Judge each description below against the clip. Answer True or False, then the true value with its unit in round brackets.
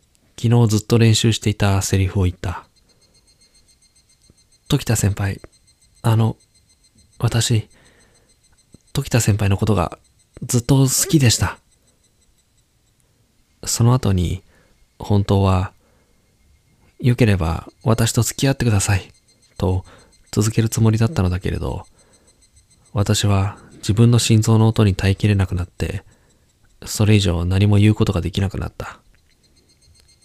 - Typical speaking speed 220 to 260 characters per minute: True (230 characters per minute)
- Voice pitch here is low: True (105 Hz)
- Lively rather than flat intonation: False (3.0 semitones)